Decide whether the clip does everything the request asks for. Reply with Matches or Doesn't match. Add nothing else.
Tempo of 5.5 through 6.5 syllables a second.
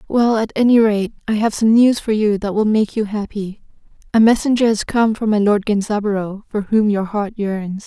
Doesn't match